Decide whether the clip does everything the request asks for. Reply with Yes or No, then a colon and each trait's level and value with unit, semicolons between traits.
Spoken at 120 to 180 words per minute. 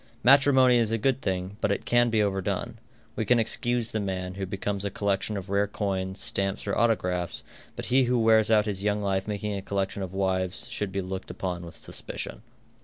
No: fast, 205 wpm